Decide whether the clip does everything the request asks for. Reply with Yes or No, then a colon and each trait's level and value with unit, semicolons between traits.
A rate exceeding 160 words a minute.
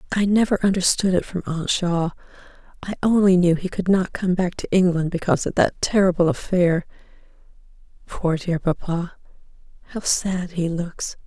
No: average, 155 wpm